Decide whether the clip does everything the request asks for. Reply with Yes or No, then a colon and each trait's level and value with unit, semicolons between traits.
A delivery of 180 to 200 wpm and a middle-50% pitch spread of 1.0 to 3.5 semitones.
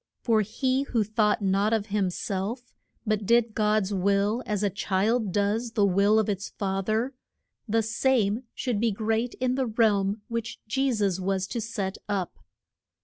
No: average, 170 wpm; narrow, 2.5 semitones